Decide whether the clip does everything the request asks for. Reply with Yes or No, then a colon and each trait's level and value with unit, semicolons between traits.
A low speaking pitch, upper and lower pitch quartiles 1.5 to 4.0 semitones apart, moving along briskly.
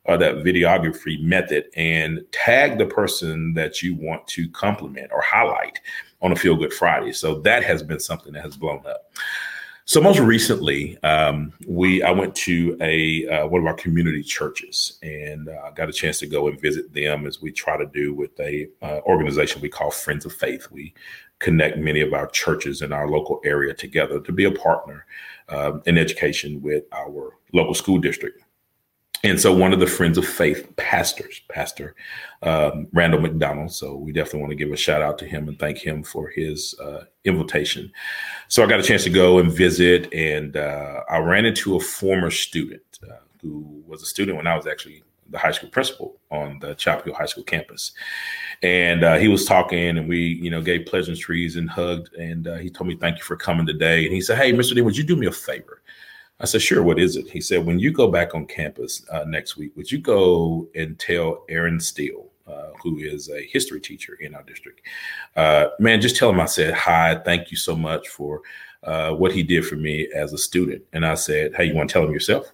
Yes: very low, 85 Hz; average, 3.3 semitones; fast, 215 wpm